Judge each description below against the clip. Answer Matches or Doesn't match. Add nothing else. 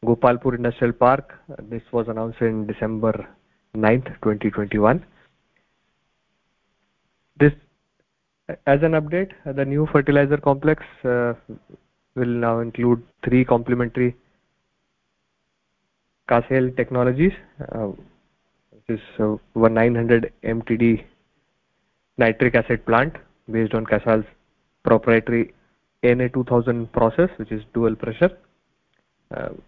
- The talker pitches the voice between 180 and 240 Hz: Doesn't match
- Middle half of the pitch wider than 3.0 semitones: Doesn't match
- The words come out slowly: Matches